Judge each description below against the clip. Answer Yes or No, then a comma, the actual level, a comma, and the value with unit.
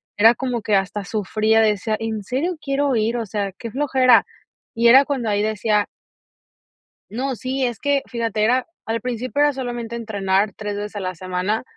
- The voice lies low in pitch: No, high, 225 Hz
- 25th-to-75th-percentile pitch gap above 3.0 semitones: Yes, average, 3.5 semitones